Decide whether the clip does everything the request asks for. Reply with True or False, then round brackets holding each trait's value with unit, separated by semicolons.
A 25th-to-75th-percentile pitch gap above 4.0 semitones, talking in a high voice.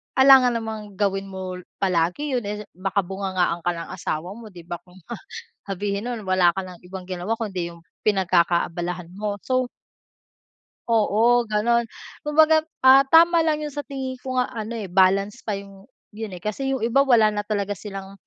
True (4.5 semitones; 205 Hz)